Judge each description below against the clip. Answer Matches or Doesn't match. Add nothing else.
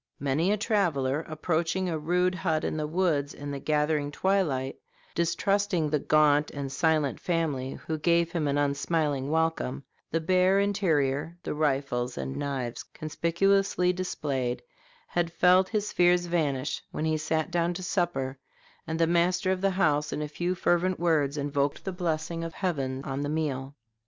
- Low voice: Doesn't match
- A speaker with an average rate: Matches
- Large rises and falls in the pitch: Doesn't match